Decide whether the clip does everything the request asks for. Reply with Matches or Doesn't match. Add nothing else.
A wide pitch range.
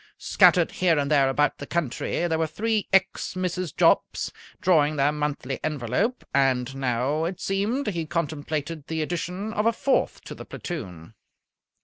Doesn't match